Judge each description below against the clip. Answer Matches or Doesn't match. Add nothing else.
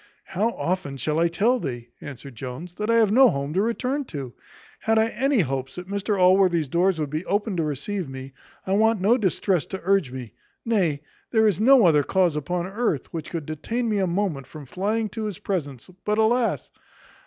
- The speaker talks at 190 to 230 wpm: Matches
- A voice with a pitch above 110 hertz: Matches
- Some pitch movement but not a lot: Doesn't match